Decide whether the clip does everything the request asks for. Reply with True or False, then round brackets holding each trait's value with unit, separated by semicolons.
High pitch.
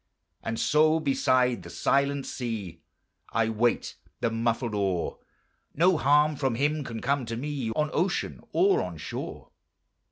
False (135 Hz)